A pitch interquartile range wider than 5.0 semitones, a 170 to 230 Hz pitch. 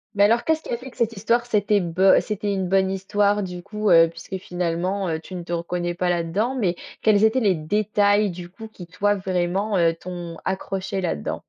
No: average, 3.0 semitones; high, 190 Hz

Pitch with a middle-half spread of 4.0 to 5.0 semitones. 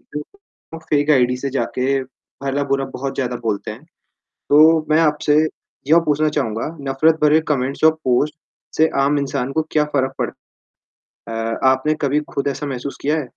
No: average, 2.7 semitones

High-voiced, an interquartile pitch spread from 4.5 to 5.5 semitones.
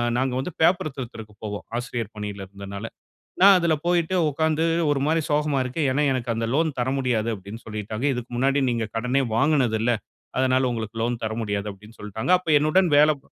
No: low, 125 Hz; average, 5.1 semitones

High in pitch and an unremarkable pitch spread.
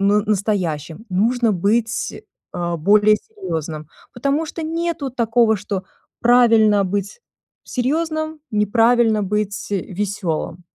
Yes: high, 215 Hz; average, 3.9 semitones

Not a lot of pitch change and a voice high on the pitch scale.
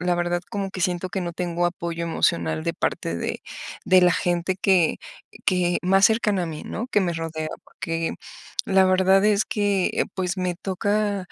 No: narrow, 2.0 semitones; medium, 180 Hz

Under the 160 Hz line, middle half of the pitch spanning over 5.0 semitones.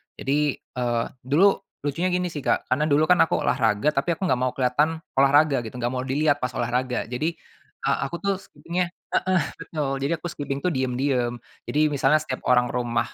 No: medium, 140 Hz; average, 3.8 semitones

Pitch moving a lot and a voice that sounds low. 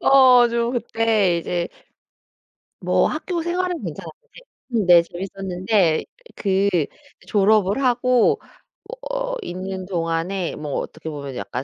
No: wide, 5.8 semitones; high, 195 Hz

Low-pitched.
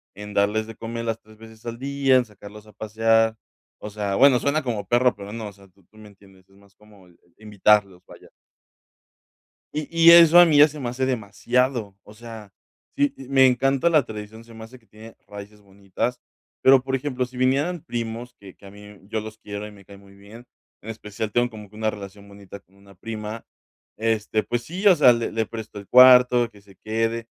Yes: low, 110 Hz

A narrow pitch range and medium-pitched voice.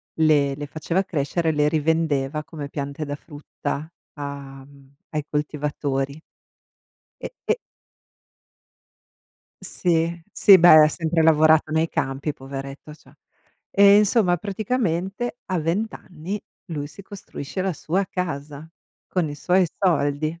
No: average, 3.7 semitones; medium, 155 Hz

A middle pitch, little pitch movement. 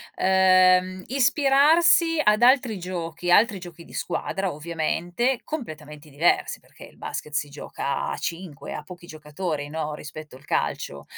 No: medium, 175 Hz; wide, 5.6 semitones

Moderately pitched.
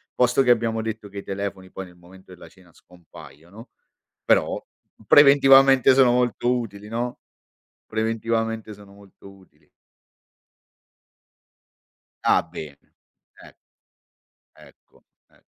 No: low, 110 Hz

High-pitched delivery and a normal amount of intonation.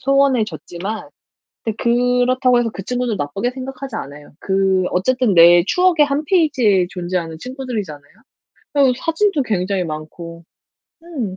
No: high, 230 Hz; wide, 6.5 semitones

